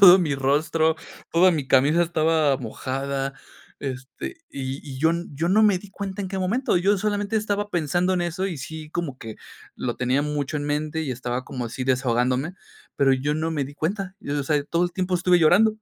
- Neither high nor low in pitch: Yes, medium, 155 Hz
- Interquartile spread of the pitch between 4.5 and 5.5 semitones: Yes, average, 5.0 semitones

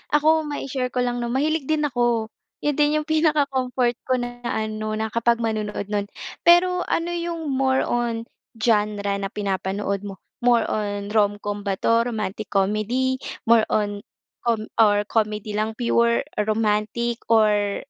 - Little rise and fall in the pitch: No, average, 3.8 semitones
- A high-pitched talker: Yes, high, 230 Hz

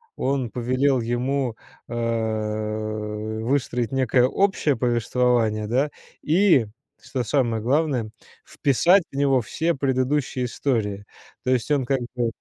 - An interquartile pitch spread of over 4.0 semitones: No, average, 3.6 semitones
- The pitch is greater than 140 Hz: No, low, 125 Hz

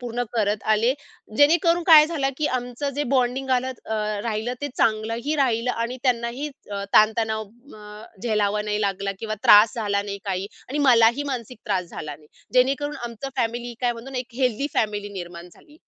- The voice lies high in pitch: Yes, high, 235 Hz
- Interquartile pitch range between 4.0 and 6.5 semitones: No, average, 3.6 semitones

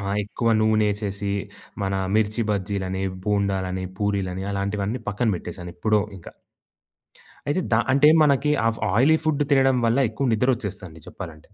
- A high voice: No, low, 105 Hz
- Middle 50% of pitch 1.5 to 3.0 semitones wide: No, average, 3.4 semitones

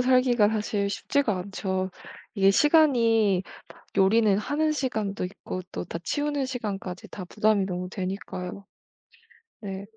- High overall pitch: Yes, high, 205 Hz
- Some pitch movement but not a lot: Yes, average, 4.6 semitones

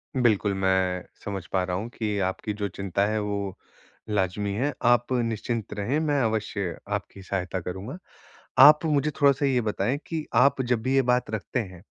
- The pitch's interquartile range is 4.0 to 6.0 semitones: Yes, average, 4.5 semitones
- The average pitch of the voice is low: Yes, low, 110 Hz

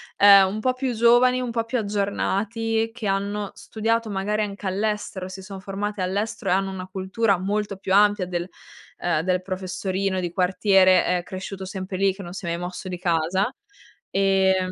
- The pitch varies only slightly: Yes, narrow, 2.1 semitones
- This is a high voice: Yes, high, 195 Hz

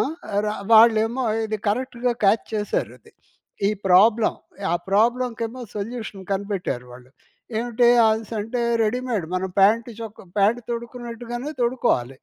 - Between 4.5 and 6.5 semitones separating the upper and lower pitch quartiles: No, average, 2.8 semitones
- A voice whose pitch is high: Yes, high, 225 Hz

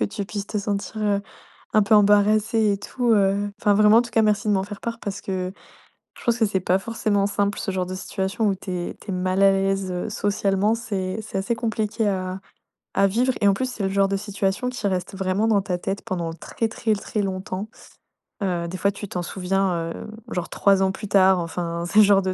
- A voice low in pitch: No, high, 200 Hz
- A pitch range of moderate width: No, narrow, 2.1 semitones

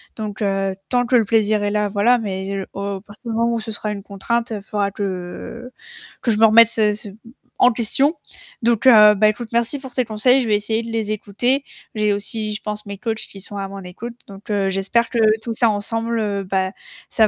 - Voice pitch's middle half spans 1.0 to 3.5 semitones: Yes, narrow, 2.4 semitones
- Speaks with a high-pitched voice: Yes, high, 215 Hz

